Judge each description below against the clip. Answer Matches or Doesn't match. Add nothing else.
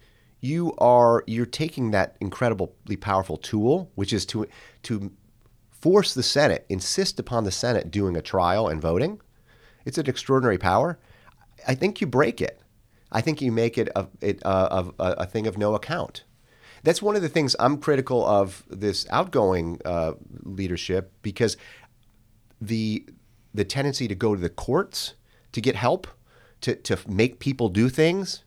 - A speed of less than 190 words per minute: Matches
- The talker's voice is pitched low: Matches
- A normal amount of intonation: Matches